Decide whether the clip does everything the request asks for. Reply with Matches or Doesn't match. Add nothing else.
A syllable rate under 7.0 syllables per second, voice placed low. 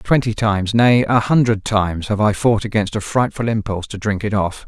Matches